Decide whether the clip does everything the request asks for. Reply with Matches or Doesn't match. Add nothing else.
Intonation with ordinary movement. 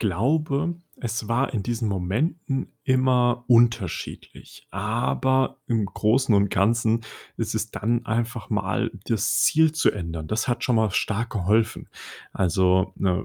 Matches